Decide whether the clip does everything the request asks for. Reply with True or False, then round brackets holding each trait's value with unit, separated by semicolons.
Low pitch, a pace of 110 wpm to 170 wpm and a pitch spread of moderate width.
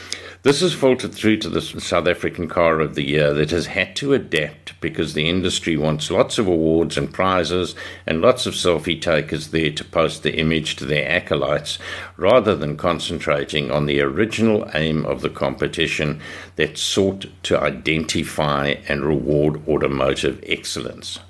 True (80 Hz; 160 wpm; 3.4 semitones)